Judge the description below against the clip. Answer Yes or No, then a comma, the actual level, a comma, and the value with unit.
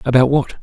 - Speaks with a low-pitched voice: Yes, low, 130 Hz